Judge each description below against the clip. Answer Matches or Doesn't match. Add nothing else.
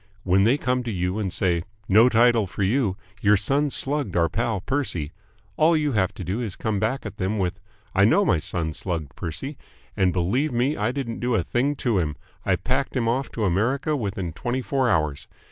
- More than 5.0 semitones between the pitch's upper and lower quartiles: Matches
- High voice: Doesn't match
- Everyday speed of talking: Doesn't match